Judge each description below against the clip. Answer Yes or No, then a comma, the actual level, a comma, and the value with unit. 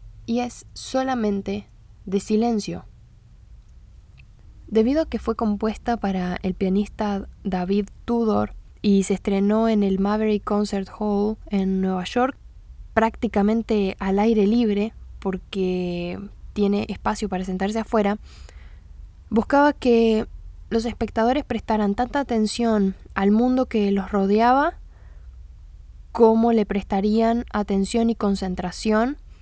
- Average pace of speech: No, slow, 110 wpm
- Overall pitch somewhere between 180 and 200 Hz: No, high, 210 Hz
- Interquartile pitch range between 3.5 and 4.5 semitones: No, average, 2.8 semitones